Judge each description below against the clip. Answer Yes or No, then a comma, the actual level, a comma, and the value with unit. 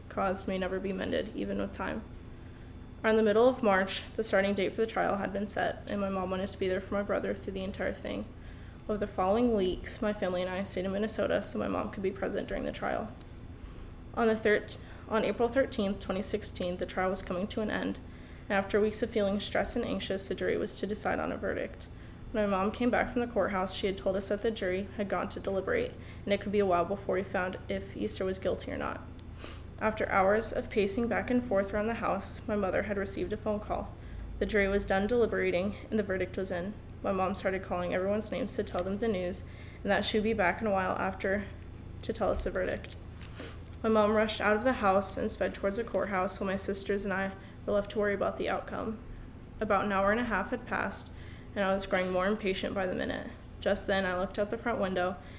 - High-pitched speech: Yes, high, 195 Hz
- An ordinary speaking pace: No, fast, 240 wpm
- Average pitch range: No, narrow, 2.2 semitones